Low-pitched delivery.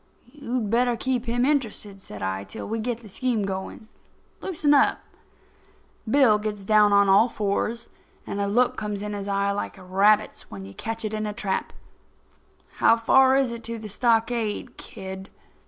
No: high, 215 Hz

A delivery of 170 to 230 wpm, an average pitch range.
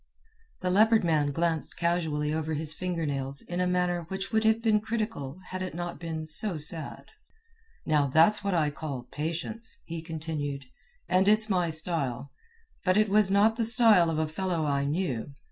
Yes: average, 180 wpm; average, 4.1 semitones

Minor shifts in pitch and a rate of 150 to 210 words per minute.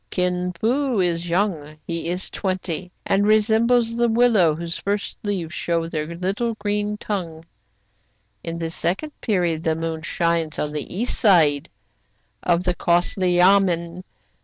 No: average, 3.6 semitones; average, 155 wpm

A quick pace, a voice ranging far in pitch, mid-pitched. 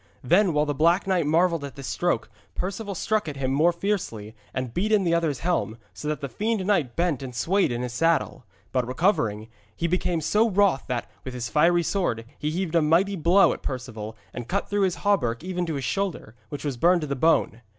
Yes: fast, 220 wpm; wide, 6.1 semitones; medium, 165 Hz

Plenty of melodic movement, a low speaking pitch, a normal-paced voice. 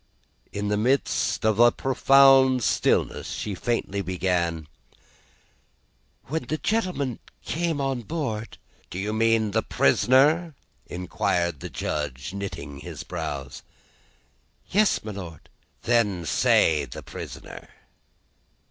No: wide, 7.1 semitones; low, 110 Hz; slow, 110 wpm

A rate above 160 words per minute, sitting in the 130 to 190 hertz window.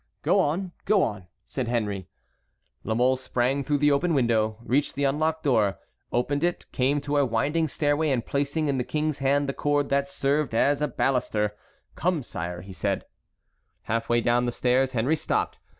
Yes: average, 180 wpm; low, 135 Hz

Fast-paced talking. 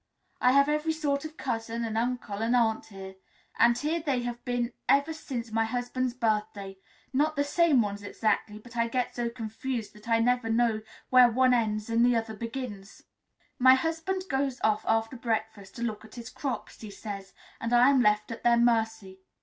No: average, 190 wpm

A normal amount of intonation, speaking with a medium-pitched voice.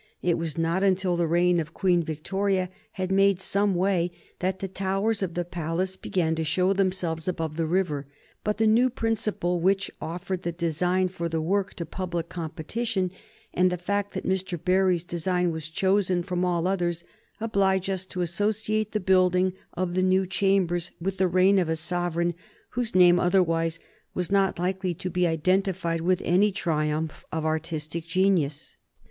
No: narrow, 2.2 semitones; medium, 180 Hz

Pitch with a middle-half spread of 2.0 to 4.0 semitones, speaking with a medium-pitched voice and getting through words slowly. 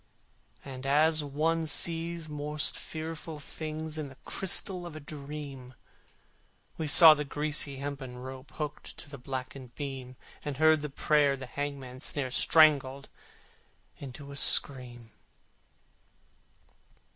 Yes: narrow, 2.6 semitones; medium, 145 Hz; slow, 120 wpm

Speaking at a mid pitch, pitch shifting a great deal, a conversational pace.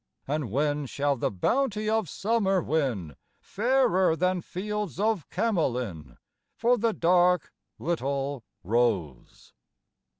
No: medium, 170 Hz; wide, 7.7 semitones; slow, 105 wpm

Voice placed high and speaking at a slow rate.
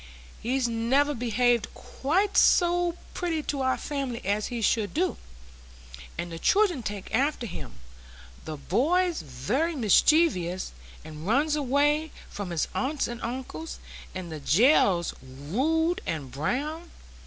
Yes: high, 245 Hz; slow, 125 wpm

